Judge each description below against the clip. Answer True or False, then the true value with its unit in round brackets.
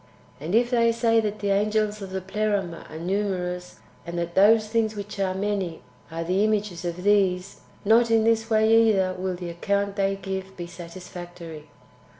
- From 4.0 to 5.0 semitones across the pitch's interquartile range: False (3.2 semitones)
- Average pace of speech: True (180 wpm)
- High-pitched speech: True (195 Hz)